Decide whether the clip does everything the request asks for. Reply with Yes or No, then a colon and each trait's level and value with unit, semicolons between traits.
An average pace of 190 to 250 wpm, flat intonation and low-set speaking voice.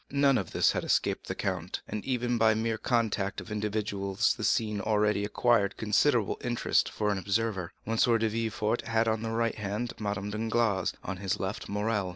Yes: average, 195 wpm; narrow, 2.2 semitones; low, 110 Hz